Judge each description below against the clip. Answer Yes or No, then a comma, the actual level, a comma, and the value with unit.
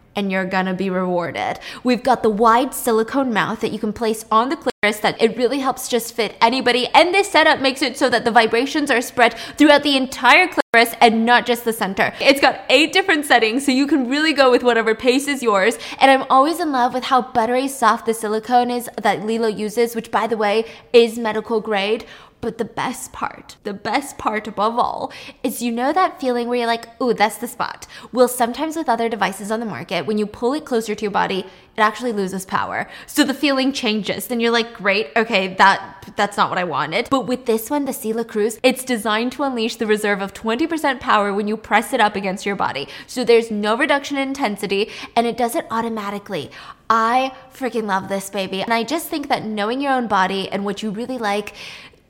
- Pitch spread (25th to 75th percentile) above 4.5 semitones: No, average, 3.3 semitones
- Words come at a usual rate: No, fast, 220 wpm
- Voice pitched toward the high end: Yes, high, 230 Hz